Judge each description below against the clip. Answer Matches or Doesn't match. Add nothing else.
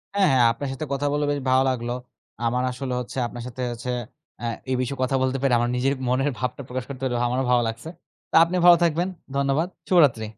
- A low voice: Matches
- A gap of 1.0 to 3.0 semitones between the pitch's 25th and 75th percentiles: Matches